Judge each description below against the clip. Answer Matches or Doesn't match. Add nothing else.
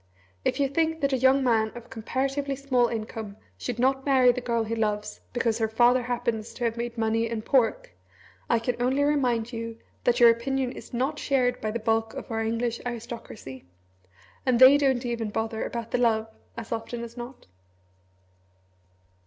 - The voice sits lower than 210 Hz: Doesn't match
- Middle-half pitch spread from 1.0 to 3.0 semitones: Matches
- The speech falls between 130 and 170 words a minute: Doesn't match